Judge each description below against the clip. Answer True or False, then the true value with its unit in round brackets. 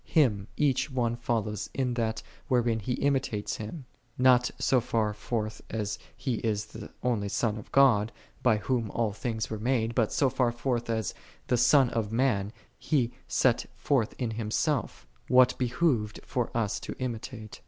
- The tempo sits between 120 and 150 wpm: False (165 wpm)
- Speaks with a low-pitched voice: True (115 Hz)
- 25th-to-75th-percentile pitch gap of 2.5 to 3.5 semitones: True (2.9 semitones)